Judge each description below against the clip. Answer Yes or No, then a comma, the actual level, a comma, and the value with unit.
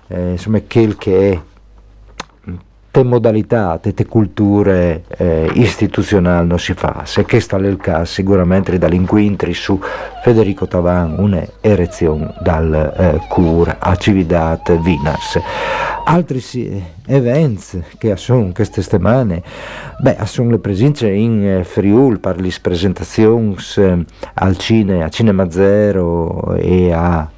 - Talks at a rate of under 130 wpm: Yes, average, 120 wpm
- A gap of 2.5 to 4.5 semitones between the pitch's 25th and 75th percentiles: Yes, average, 3.4 semitones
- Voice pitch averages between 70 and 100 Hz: Yes, very low, 95 Hz